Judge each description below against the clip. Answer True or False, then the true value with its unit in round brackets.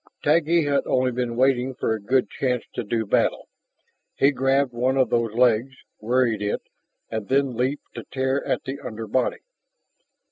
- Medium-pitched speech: False (125 Hz)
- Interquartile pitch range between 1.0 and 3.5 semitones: True (2.5 semitones)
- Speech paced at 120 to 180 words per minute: True (170 wpm)